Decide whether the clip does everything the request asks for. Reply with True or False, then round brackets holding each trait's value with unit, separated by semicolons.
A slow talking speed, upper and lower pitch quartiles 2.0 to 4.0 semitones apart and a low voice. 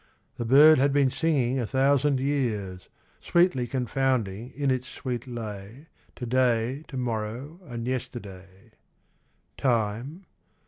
True (120 wpm; 3.4 semitones; 125 Hz)